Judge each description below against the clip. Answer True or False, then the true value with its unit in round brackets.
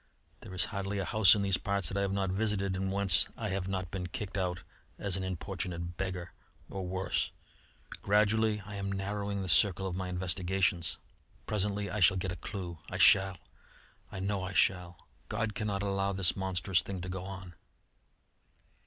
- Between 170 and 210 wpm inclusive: True (180 wpm)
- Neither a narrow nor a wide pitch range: False (1.6 semitones)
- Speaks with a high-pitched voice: False (95 Hz)